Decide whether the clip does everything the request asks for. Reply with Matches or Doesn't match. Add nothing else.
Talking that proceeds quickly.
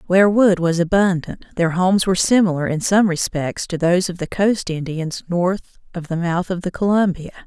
Doesn't match